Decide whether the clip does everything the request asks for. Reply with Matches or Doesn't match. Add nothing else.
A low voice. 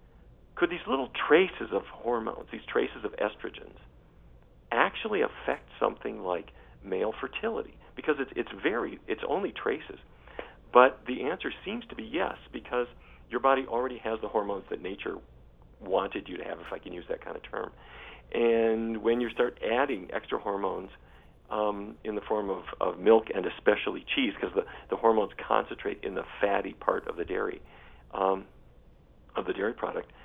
Matches